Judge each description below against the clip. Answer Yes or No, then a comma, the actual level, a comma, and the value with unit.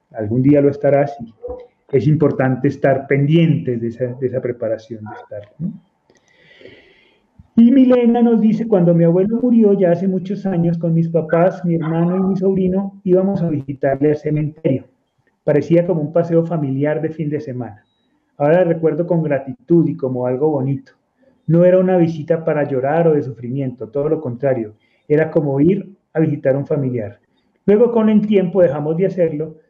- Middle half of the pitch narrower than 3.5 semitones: No, average, 5.0 semitones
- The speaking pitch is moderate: Yes, medium, 160 Hz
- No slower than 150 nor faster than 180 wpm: Yes, average, 170 wpm